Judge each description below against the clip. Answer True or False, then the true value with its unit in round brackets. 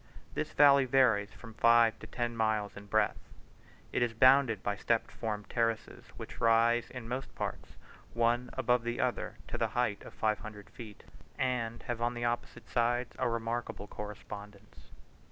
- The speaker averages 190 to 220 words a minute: False (165 wpm)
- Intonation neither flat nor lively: False (2.0 semitones)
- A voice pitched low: True (115 Hz)